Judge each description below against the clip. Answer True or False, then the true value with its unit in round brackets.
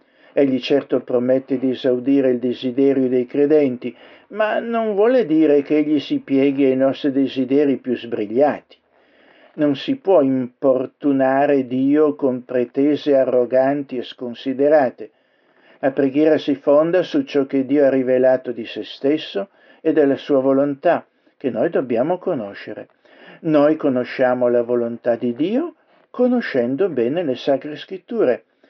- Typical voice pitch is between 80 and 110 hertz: False (140 Hz)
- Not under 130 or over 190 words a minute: True (135 wpm)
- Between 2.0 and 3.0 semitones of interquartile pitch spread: True (2.6 semitones)